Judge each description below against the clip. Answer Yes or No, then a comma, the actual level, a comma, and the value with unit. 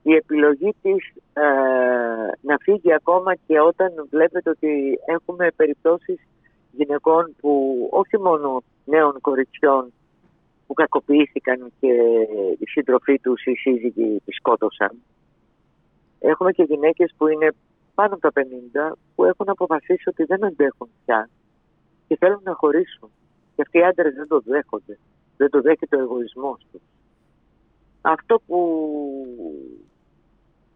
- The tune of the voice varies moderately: Yes, average, 4.6 semitones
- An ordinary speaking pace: Yes, average, 125 wpm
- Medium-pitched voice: Yes, medium, 150 Hz